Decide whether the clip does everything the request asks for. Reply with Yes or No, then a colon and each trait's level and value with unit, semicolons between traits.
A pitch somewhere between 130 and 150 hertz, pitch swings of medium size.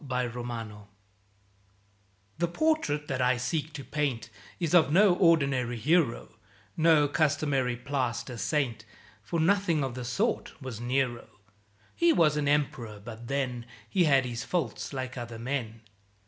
Yes: low, 135 Hz; average, 4.4 semitones